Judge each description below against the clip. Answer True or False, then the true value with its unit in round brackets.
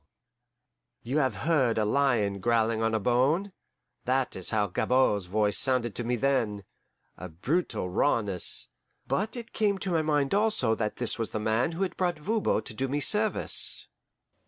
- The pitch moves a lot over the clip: True (6.4 semitones)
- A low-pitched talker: True (125 Hz)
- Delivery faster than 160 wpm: True (170 wpm)